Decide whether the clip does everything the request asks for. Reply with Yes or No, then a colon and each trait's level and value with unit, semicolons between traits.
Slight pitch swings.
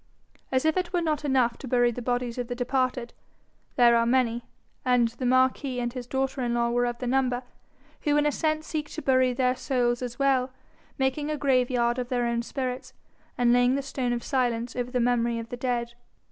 Yes: narrow, 1.7 semitones